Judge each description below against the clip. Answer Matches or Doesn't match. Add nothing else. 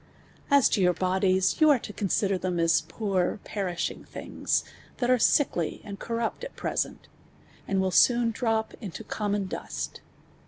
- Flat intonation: Doesn't match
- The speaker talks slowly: Doesn't match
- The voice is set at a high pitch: Matches